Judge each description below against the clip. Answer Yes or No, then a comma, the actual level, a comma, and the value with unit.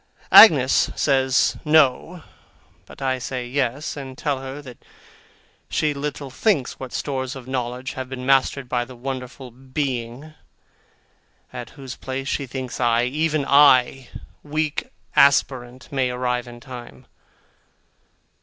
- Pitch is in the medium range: No, low, 130 Hz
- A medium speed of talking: No, slow, 125 wpm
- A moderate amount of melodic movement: No, narrow, 2.0 semitones